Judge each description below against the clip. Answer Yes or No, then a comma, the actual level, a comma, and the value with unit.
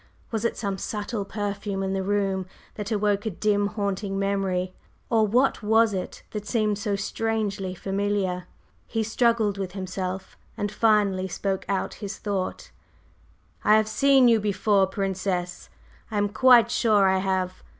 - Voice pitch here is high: Yes, high, 205 Hz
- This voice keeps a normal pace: Yes, average, 150 wpm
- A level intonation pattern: Yes, narrow, 2.0 semitones